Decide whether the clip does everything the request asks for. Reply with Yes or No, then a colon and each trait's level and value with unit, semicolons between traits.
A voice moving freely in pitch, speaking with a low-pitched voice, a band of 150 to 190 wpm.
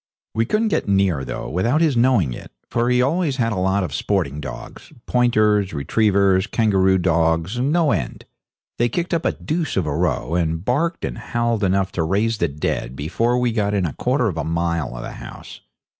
No: wide, 6.3 semitones; low, 100 Hz; average, 200 wpm